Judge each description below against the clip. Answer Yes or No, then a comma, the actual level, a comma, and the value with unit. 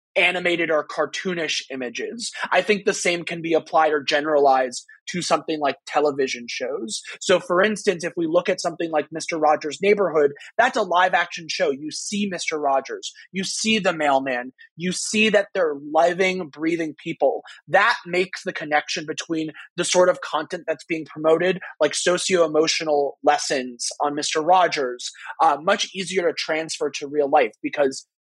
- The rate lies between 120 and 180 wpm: Yes, average, 165 wpm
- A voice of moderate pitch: Yes, medium, 165 Hz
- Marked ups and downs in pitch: No, average, 3.7 semitones